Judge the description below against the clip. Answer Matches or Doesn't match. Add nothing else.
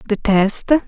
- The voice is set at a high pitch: Matches